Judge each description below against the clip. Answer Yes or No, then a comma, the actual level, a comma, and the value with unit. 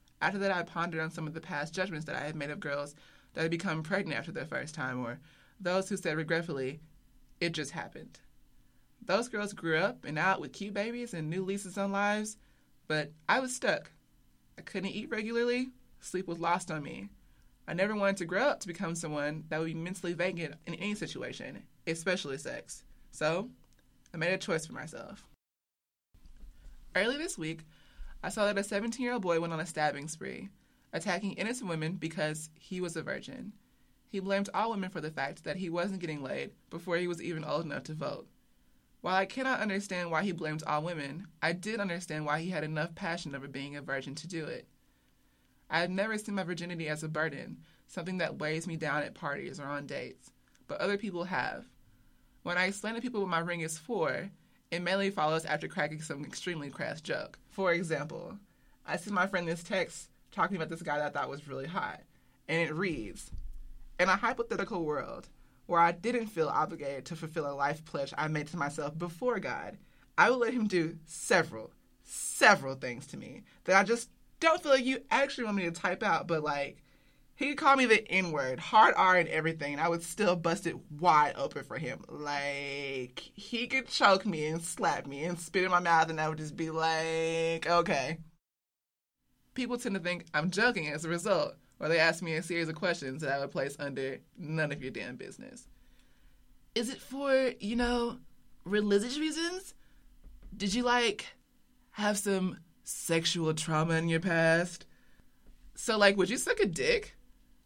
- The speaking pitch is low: No, medium, 170 Hz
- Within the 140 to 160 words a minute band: No, average, 195 wpm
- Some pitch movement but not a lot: Yes, average, 4.2 semitones